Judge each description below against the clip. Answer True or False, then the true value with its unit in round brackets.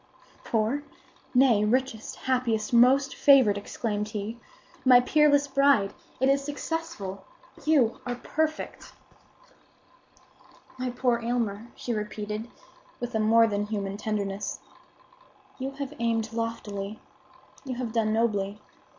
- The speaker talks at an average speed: False (115 wpm)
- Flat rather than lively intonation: False (3.8 semitones)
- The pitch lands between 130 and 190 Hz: False (230 Hz)